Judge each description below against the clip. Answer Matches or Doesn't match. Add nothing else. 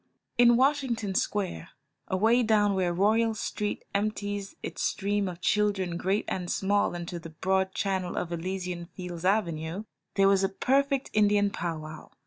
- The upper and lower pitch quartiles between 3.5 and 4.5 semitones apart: Doesn't match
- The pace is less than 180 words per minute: Matches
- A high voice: Matches